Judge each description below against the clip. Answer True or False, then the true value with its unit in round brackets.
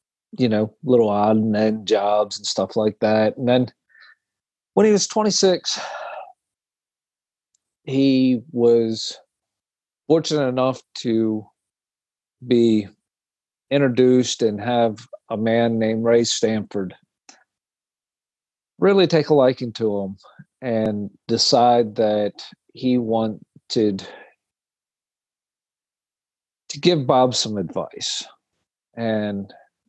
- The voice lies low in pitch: True (115 Hz)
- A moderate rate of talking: False (95 wpm)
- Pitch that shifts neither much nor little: True (3.0 semitones)